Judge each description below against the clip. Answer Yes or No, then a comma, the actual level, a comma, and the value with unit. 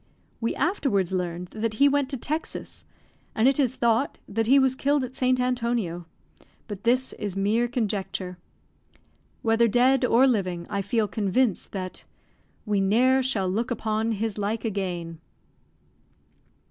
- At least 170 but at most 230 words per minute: No, average, 145 wpm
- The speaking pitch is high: Yes, high, 225 Hz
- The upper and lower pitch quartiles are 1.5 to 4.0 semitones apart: No, average, 4.4 semitones